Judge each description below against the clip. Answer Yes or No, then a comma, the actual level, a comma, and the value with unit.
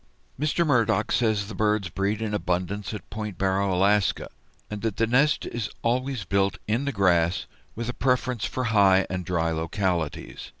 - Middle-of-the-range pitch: No, low, 105 Hz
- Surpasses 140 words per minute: Yes, average, 170 wpm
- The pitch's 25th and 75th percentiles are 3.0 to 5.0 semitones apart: Yes, average, 3.5 semitones